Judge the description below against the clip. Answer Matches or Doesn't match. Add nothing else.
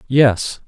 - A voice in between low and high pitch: Doesn't match